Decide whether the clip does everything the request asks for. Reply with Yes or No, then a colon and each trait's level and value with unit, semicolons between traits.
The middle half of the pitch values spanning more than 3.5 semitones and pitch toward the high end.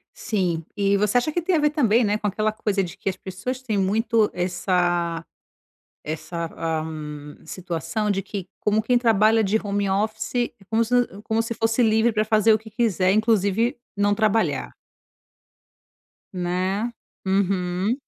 No: average, 3.2 semitones; high, 210 Hz